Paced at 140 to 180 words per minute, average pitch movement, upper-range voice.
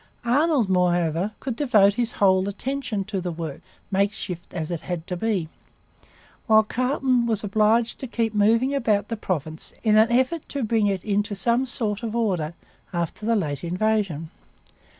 Yes: average, 165 wpm; average, 4.4 semitones; high, 210 Hz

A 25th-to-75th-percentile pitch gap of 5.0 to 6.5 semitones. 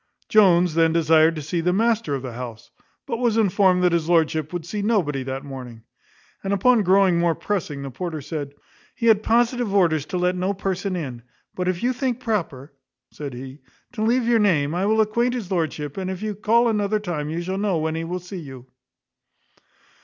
Yes: wide, 5.4 semitones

